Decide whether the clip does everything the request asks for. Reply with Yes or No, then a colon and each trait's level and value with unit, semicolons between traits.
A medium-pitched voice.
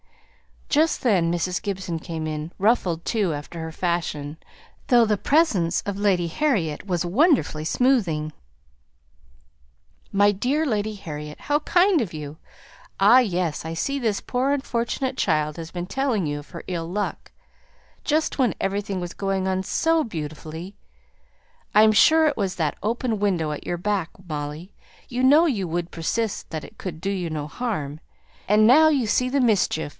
No: high, 195 Hz